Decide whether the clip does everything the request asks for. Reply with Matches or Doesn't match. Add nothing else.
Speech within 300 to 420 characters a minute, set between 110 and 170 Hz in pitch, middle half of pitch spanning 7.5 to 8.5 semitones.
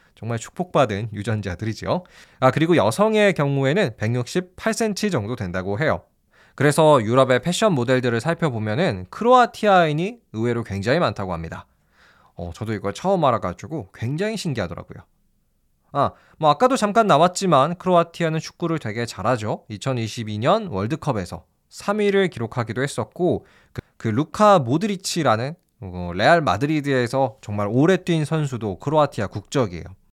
Matches